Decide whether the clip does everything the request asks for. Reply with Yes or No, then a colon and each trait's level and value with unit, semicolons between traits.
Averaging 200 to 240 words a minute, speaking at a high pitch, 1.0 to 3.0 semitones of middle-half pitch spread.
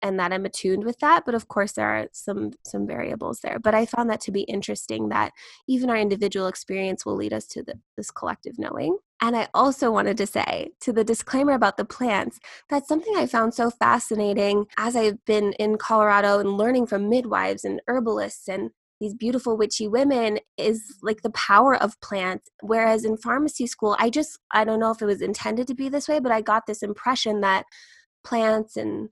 No: fast, 205 wpm; high, 220 Hz; average, 3.5 semitones